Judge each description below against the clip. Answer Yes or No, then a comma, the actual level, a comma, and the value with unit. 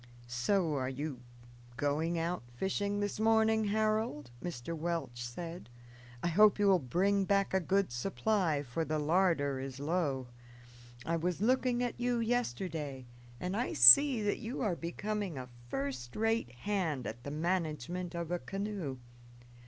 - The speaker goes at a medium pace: Yes, average, 150 wpm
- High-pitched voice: No, medium, 170 Hz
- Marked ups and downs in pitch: Yes, wide, 6.4 semitones